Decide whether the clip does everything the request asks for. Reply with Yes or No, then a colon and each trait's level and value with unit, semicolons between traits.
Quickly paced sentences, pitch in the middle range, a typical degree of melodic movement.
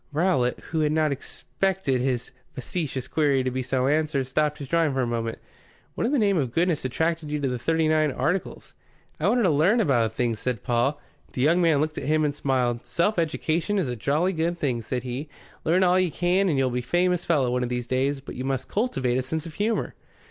Yes: fast, 230 wpm; medium, 150 Hz; average, 4.7 semitones